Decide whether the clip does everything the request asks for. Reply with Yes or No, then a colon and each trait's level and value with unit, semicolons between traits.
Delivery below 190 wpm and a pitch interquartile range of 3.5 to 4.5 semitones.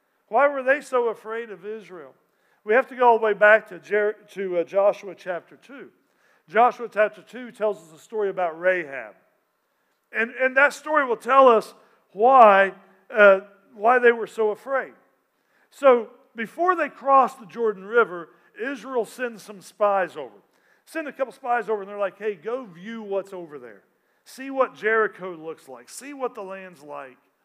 Yes: average, 175 wpm; average, 4.1 semitones